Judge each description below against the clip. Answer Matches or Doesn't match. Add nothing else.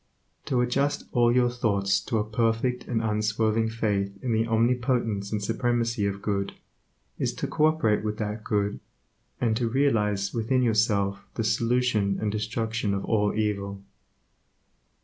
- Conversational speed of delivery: Matches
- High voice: Doesn't match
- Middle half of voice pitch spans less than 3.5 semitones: Matches